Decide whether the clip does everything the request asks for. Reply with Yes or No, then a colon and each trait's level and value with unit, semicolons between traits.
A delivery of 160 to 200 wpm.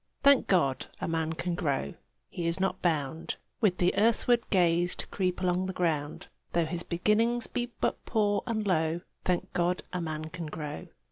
Yes: average, 175 wpm